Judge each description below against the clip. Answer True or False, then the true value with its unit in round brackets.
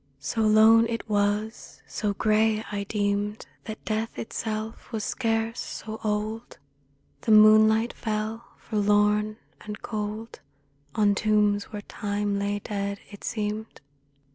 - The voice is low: False (215 Hz)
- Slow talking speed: True (120 wpm)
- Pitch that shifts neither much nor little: False (1.1 semitones)